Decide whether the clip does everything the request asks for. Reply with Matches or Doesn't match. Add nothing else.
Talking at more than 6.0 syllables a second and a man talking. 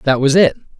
Matches